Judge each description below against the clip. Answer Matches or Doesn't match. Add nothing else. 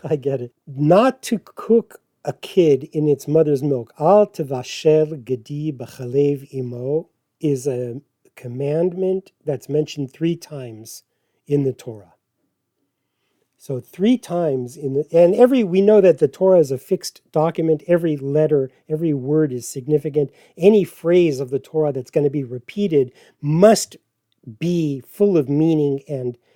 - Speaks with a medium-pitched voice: Matches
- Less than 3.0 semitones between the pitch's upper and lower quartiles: Doesn't match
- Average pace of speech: Matches